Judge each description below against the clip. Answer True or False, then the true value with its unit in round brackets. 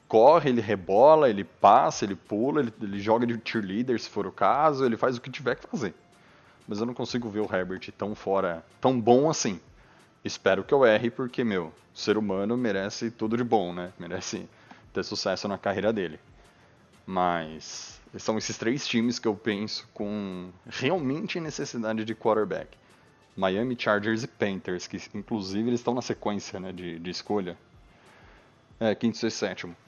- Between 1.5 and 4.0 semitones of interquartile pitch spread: True (3.6 semitones)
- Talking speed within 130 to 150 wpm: False (170 wpm)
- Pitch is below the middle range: True (110 Hz)